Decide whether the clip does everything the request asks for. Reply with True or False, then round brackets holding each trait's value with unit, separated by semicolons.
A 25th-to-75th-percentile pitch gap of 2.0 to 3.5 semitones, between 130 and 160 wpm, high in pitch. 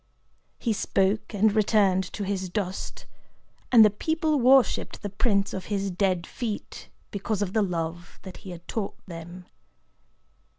True (2.8 semitones; 145 wpm; 200 Hz)